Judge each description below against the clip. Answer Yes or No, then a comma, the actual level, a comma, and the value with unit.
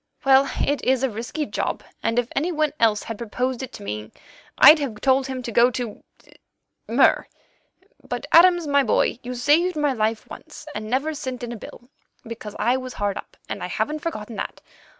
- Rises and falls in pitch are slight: No, average, 3.9 semitones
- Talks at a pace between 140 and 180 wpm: No, average, 190 wpm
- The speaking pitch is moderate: No, very high, 255 Hz